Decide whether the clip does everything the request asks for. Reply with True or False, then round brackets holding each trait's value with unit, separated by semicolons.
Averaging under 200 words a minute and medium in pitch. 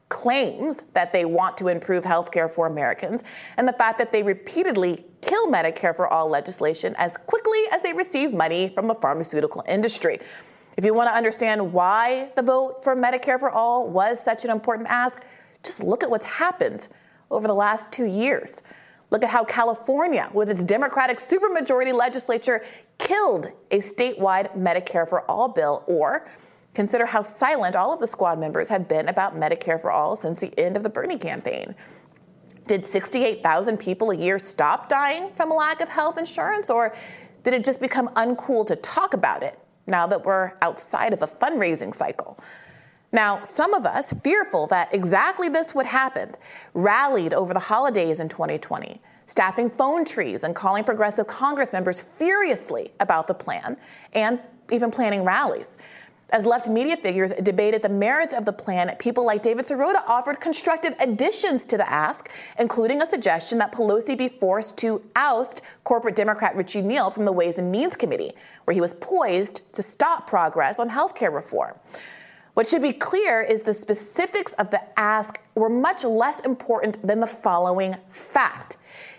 False (170 wpm; 230 Hz)